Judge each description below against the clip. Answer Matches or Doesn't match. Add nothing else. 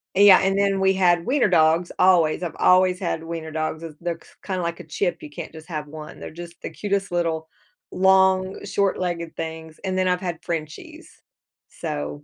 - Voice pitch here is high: Doesn't match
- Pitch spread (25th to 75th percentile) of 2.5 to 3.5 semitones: Matches